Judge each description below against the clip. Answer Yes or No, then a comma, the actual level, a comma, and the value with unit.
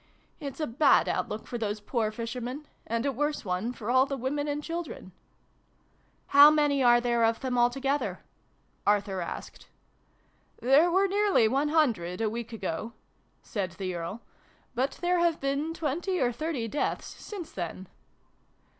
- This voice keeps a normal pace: Yes, average, 165 wpm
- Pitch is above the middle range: Yes, very high, 255 Hz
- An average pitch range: Yes, average, 5.0 semitones